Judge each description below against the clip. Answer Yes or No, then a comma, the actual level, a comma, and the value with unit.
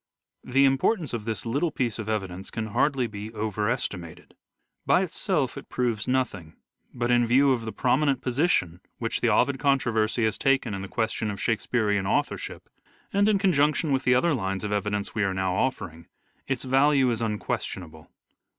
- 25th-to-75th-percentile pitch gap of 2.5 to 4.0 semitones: No, average, 4.5 semitones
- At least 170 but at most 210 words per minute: Yes, average, 180 wpm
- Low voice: Yes, low, 120 Hz